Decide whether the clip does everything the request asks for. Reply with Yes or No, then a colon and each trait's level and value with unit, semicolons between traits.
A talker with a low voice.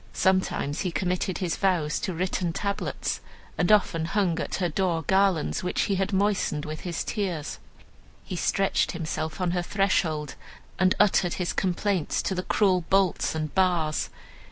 No: medium, 180 Hz